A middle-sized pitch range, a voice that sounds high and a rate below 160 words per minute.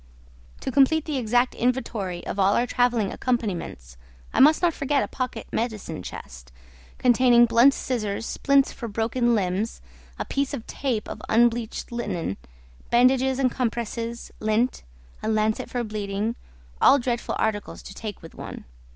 Yes: average, 3.1 semitones; high, 235 Hz; average, 150 wpm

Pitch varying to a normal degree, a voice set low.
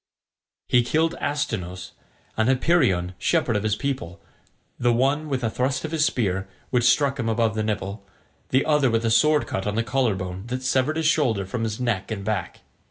Yes: average, 4.7 semitones; low, 120 Hz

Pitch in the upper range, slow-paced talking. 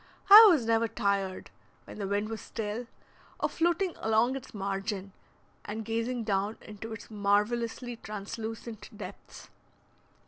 Yes: high, 220 Hz; slow, 130 wpm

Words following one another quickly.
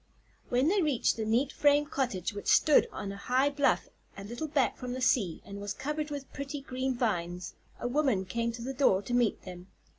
Yes: fast, 210 wpm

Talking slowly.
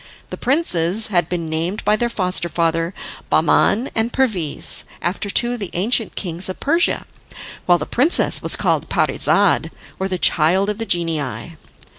No: average, 160 wpm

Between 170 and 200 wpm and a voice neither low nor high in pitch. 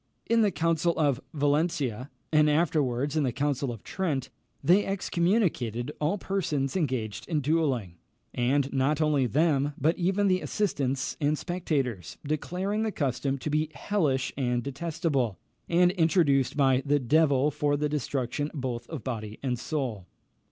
No: average, 145 wpm; medium, 145 Hz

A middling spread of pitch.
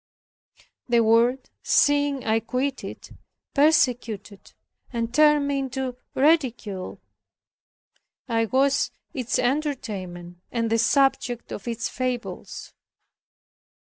Yes: average, 3.5 semitones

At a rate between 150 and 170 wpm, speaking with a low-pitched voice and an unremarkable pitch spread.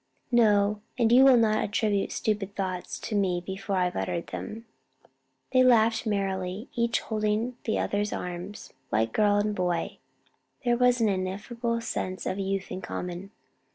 No: average, 155 wpm; high, 205 Hz; average, 3.4 semitones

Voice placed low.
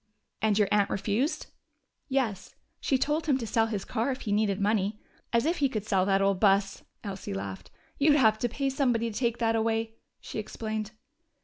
No: high, 220 Hz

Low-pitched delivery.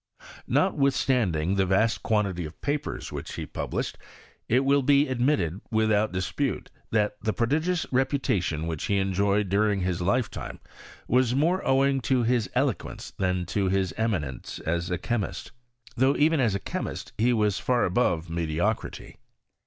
Yes: low, 110 Hz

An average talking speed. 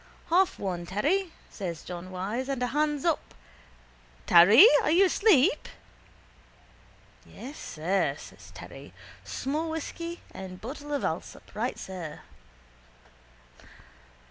No: slow, 110 wpm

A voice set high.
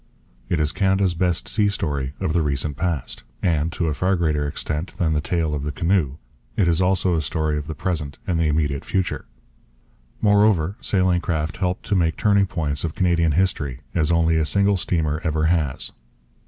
No: very low, 80 Hz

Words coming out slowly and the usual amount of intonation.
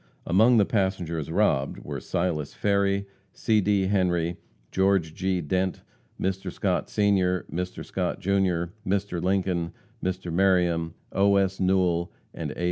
No: slow, 130 wpm; narrow, 2.1 semitones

